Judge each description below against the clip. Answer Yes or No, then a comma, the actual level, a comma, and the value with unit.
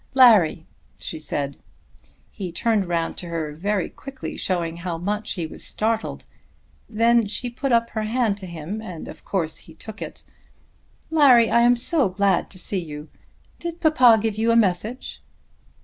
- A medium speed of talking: Yes, average, 165 wpm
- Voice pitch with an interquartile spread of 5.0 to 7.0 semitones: Yes, wide, 5.5 semitones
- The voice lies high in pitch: Yes, high, 210 Hz